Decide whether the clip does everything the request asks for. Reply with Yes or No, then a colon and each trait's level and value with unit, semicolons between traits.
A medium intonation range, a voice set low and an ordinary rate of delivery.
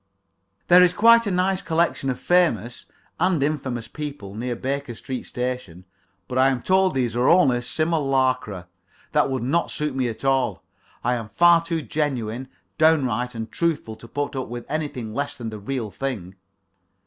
Yes: average, 4.7 semitones; low, 130 Hz; average, 170 wpm